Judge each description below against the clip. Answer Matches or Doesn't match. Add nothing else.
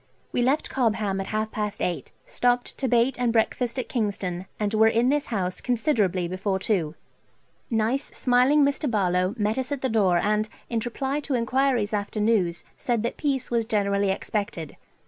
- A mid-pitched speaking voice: Doesn't match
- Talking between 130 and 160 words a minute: Doesn't match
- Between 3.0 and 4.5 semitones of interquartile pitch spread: Matches